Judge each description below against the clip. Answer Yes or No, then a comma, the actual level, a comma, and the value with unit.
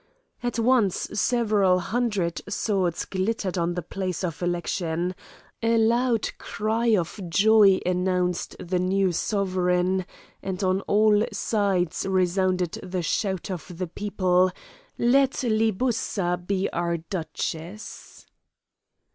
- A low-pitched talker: No, high, 190 Hz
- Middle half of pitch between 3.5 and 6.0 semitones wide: No, average, 3.1 semitones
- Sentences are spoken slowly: Yes, slow, 110 wpm